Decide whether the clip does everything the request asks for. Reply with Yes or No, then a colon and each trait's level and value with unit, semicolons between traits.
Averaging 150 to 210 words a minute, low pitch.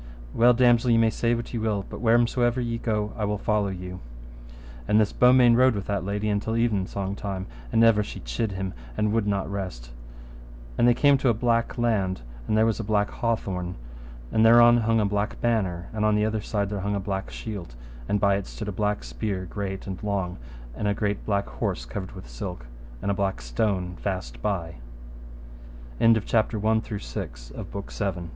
Yes: average, 175 wpm; low, 105 Hz